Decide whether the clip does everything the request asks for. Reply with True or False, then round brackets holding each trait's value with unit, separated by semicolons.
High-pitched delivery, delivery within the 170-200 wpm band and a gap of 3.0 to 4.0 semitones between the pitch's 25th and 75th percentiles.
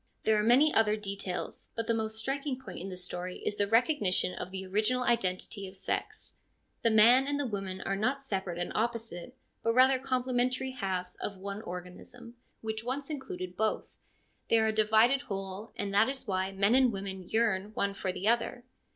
False (215 Hz; 190 wpm; 4.4 semitones)